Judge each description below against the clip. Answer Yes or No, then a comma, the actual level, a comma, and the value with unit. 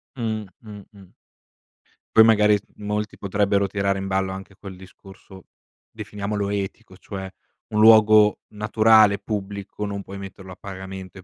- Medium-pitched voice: No, low, 100 Hz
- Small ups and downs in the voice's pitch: Yes, narrow, 1.6 semitones